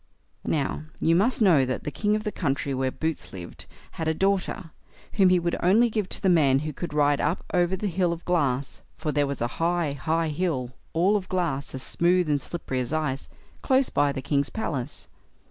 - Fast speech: Yes, fast, 210 wpm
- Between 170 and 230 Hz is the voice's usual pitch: No, medium, 160 Hz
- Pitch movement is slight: No, average, 4.6 semitones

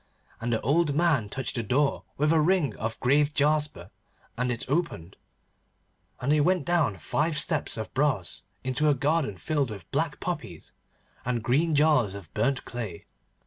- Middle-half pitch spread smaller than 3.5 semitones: No, average, 4.8 semitones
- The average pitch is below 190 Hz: Yes, medium, 140 Hz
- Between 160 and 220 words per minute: Yes, average, 165 wpm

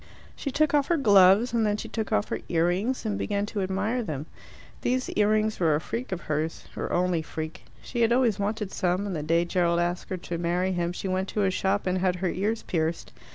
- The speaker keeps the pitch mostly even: No, average, 3.8 semitones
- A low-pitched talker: No, high, 190 Hz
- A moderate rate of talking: No, fast, 240 wpm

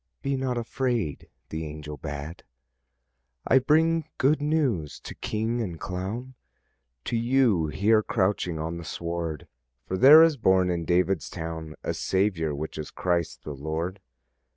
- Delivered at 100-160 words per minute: Yes, average, 145 wpm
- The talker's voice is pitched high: No, very low, 95 Hz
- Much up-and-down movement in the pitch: Yes, wide, 7.2 semitones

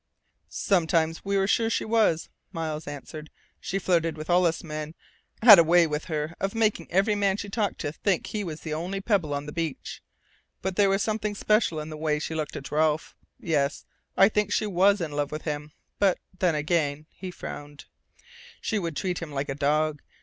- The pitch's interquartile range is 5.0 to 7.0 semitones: No, average, 4.4 semitones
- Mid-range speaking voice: Yes, medium, 165 Hz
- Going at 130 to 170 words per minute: No, fast, 205 wpm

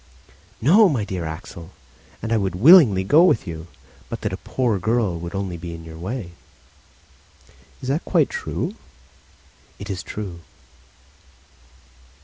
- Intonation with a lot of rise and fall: Yes, wide, 6.7 semitones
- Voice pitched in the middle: No, low, 100 Hz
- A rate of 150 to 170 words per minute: No, average, 140 wpm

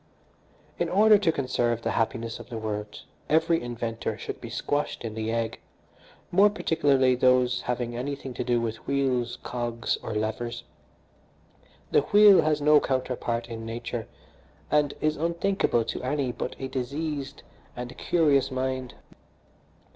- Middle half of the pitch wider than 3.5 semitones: Yes, average, 4.0 semitones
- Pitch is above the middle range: No, low, 125 Hz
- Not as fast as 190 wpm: Yes, average, 140 wpm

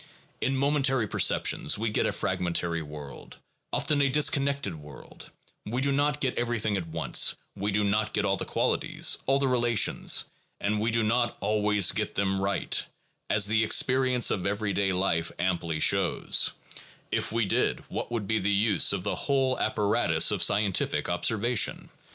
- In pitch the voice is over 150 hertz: No, low, 105 Hz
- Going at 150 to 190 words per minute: Yes, average, 165 wpm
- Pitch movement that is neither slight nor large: Yes, average, 4.4 semitones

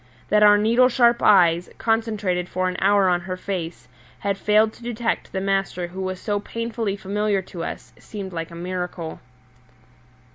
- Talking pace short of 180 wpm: Yes, average, 170 wpm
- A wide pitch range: No, average, 2.9 semitones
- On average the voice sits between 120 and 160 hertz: No, high, 195 Hz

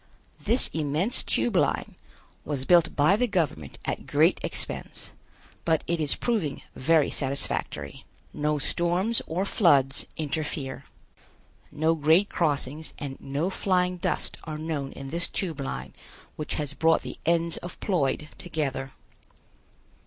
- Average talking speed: No, slow, 130 wpm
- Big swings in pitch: No, average, 3.6 semitones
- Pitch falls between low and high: Yes, medium, 155 Hz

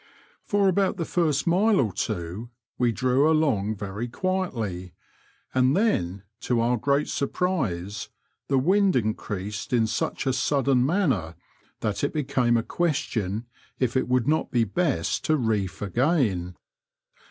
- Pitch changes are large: Yes, wide, 6.7 semitones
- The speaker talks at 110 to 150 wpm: Yes, average, 140 wpm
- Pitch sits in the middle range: No, low, 125 Hz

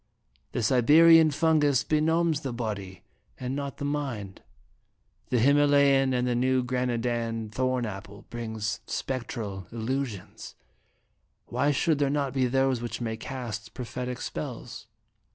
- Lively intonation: No, average, 3.5 semitones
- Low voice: Yes, low, 125 Hz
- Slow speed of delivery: Yes, slow, 130 wpm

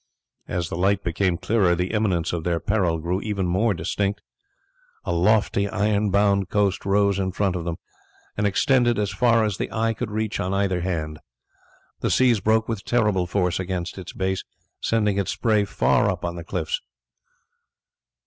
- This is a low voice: Yes, low, 100 Hz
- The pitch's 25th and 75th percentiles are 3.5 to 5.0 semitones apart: No, average, 2.9 semitones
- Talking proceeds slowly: No, average, 170 wpm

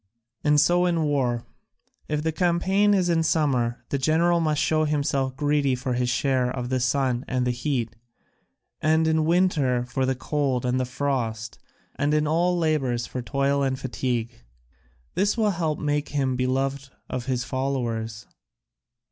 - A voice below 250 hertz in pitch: Yes, medium, 140 Hz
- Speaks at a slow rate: No, average, 165 wpm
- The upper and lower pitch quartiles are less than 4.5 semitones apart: Yes, average, 3.7 semitones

